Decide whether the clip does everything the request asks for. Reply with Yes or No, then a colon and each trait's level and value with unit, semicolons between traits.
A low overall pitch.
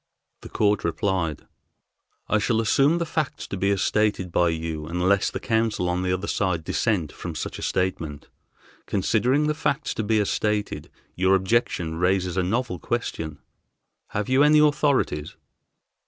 Yes: low, 100 Hz